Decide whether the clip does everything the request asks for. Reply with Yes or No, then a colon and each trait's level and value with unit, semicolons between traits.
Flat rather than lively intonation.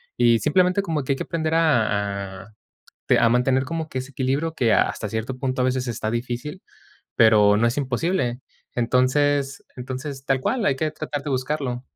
No: average, 3.7 semitones